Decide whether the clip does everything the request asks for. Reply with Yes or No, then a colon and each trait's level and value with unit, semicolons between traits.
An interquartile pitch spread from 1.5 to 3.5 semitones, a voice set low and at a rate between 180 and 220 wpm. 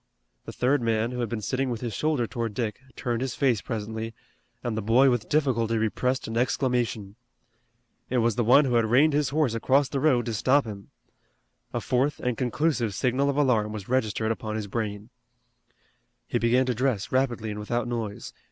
Yes: average, 2.9 semitones; low, 120 Hz; average, 190 wpm